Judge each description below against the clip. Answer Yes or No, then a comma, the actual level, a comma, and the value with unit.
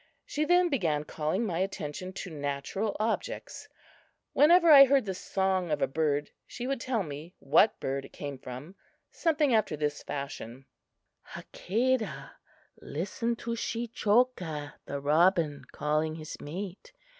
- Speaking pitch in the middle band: Yes, medium, 180 Hz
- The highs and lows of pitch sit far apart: Yes, wide, 8.0 semitones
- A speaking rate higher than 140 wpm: No, slow, 135 wpm